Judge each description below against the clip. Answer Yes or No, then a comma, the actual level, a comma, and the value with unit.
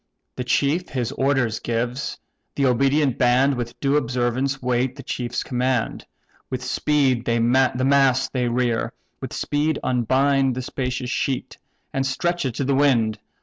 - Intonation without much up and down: Yes, narrow, 2.1 semitones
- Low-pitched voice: Yes, low, 130 Hz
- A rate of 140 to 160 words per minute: Yes, average, 150 wpm